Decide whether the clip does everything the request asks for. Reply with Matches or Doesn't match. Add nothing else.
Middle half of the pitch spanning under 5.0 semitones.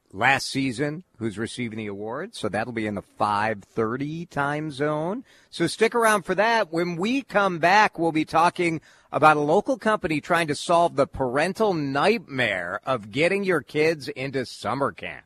Doesn't match